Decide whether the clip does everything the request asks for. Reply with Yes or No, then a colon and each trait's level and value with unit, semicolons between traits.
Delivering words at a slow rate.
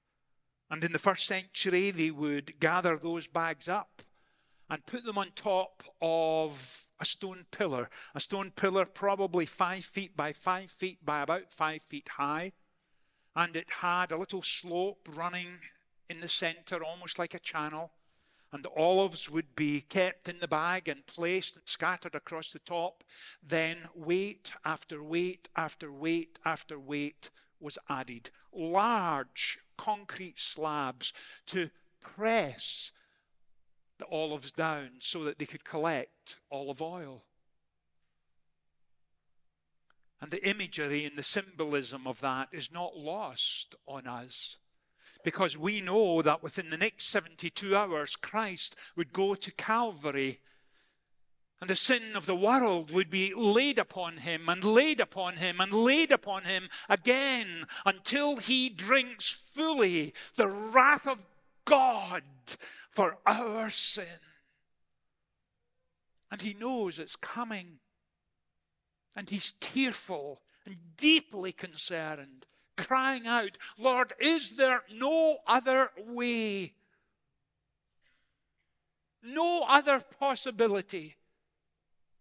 Yes: slow, 125 wpm